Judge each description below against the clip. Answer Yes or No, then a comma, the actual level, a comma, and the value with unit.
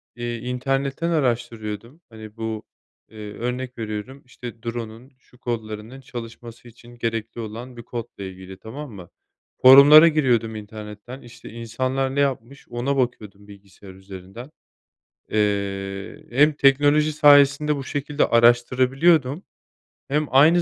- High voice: No, low, 120 Hz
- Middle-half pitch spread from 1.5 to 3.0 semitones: No, average, 3.8 semitones